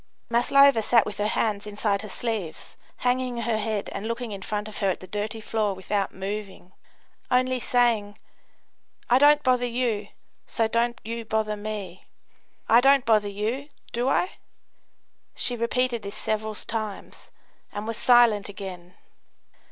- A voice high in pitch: Yes, high, 220 Hz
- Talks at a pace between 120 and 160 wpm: Yes, average, 150 wpm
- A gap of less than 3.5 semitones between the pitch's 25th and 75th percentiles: Yes, average, 2.8 semitones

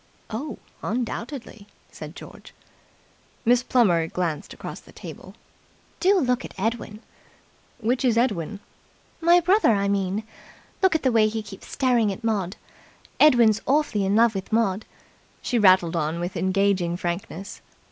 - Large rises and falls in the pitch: No, average, 4.4 semitones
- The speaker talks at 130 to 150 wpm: Yes, average, 140 wpm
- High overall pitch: Yes, high, 215 Hz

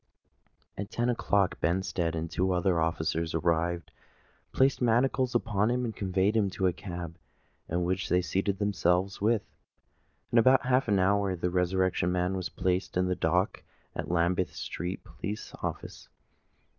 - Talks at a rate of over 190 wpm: No, average, 160 wpm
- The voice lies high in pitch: No, very low, 95 Hz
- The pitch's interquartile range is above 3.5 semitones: No, average, 2.8 semitones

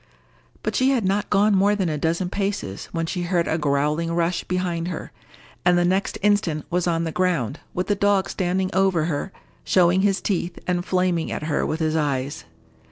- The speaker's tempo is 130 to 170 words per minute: No, average, 195 wpm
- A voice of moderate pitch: Yes, medium, 175 Hz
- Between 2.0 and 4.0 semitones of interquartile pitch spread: Yes, average, 2.7 semitones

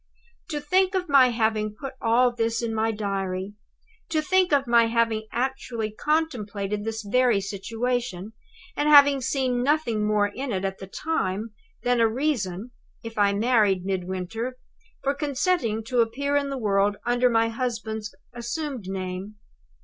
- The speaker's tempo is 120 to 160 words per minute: Yes, average, 150 wpm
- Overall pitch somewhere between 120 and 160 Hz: No, high, 230 Hz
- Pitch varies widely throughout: No, average, 4.3 semitones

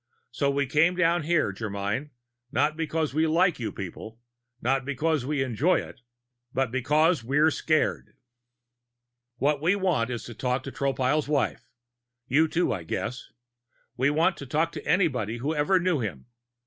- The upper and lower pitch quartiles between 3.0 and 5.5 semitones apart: Yes, average, 4.3 semitones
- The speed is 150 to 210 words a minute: Yes, average, 160 wpm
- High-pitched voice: No, medium, 140 Hz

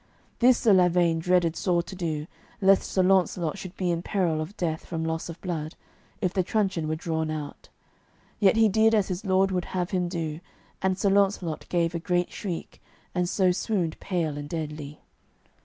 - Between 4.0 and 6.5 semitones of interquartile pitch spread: No, average, 2.8 semitones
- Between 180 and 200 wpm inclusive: Yes, average, 190 wpm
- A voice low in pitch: No, medium, 175 Hz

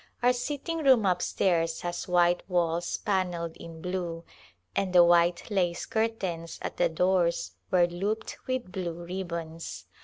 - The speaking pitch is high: No, medium, 175 Hz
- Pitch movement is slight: Yes, narrow, 2.2 semitones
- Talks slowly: No, average, 150 wpm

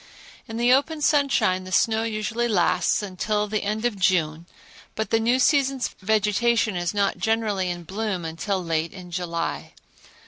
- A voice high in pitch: Yes, high, 210 Hz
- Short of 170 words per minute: Yes, average, 160 wpm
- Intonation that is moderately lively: Yes, average, 3.8 semitones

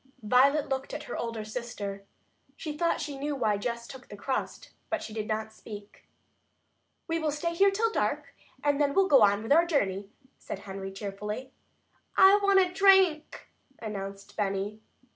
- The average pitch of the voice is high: Yes, very high, 250 Hz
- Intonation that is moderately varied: No, wide, 6.9 semitones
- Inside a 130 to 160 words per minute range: No, average, 170 wpm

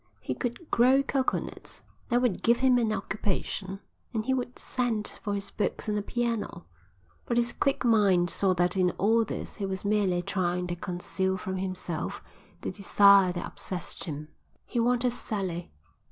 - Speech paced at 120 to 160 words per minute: No, average, 170 wpm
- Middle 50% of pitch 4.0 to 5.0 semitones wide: Yes, average, 4.5 semitones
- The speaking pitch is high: Yes, high, 200 Hz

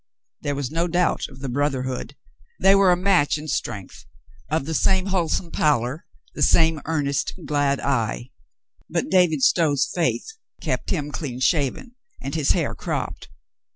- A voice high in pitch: No, medium, 150 Hz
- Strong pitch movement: No, average, 3.8 semitones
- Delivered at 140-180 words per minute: Yes, average, 155 wpm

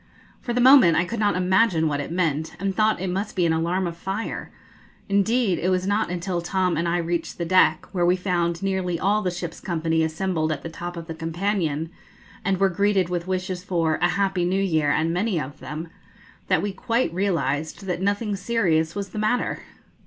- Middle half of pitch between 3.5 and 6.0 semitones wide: No, average, 3.0 semitones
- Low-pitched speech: No, medium, 180 Hz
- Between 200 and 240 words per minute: Yes, fast, 205 wpm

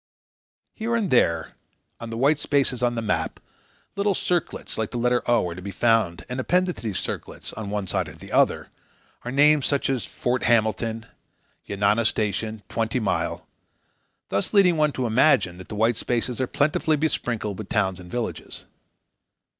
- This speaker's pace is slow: No, average, 175 wpm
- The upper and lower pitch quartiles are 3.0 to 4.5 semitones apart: No, average, 4.9 semitones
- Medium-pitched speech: No, low, 115 Hz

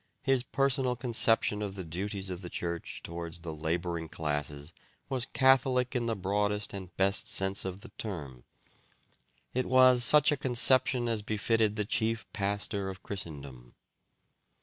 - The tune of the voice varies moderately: No, wide, 5.9 semitones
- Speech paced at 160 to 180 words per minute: No, average, 150 wpm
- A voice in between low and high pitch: No, low, 100 Hz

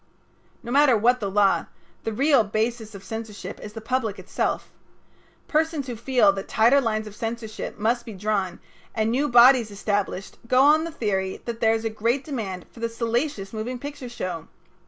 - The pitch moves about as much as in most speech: Yes, average, 3.2 semitones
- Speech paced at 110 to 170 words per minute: No, average, 180 wpm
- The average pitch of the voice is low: No, high, 225 Hz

